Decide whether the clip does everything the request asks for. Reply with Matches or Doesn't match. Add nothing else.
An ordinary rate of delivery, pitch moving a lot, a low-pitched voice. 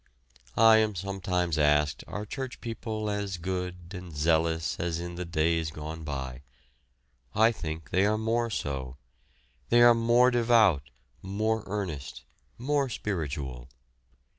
Doesn't match